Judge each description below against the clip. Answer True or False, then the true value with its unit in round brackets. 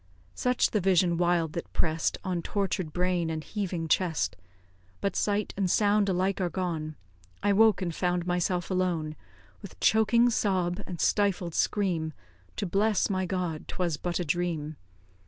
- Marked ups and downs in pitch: False (2.7 semitones)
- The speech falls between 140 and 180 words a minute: True (155 wpm)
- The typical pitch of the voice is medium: True (180 Hz)